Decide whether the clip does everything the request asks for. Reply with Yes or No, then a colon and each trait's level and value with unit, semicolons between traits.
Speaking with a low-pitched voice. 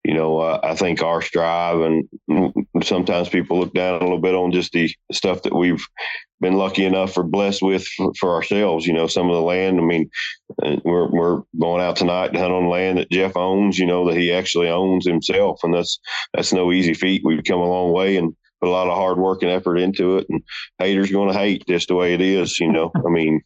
Yes: very low, 90 Hz